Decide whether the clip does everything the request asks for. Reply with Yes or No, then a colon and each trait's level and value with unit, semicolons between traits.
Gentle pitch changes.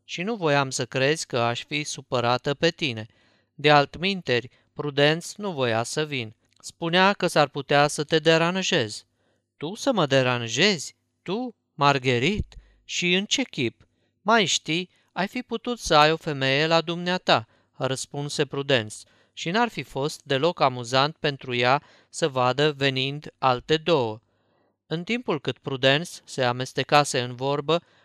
No: average, 5.0 semitones